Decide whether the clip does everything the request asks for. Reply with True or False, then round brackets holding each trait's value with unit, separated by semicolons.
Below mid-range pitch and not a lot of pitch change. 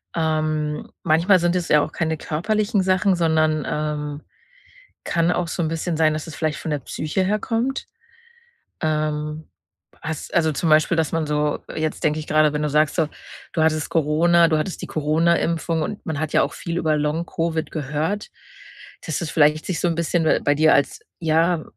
False (160 Hz; 1.9 semitones)